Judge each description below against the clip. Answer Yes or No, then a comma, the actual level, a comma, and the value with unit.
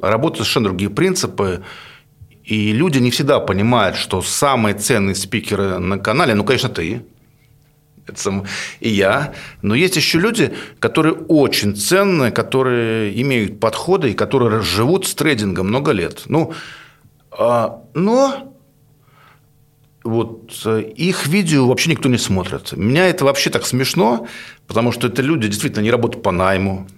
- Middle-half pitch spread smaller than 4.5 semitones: No, average, 5.2 semitones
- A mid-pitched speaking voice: No, low, 120 Hz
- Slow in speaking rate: No, average, 140 wpm